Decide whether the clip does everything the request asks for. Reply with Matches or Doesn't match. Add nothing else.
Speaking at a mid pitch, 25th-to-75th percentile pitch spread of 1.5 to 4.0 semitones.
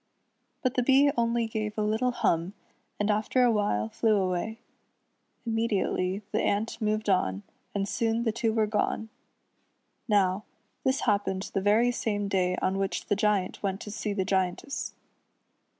Doesn't match